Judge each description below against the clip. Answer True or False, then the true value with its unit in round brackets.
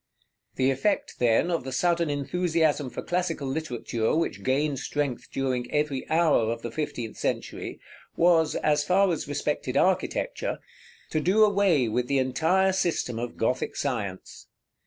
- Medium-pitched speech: True (145 Hz)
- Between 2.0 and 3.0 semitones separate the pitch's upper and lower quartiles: False (5.1 semitones)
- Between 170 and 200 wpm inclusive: False (155 wpm)